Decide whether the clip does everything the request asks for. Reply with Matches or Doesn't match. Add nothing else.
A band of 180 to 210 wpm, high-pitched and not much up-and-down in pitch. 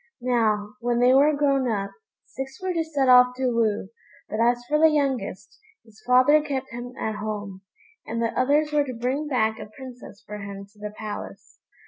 Doesn't match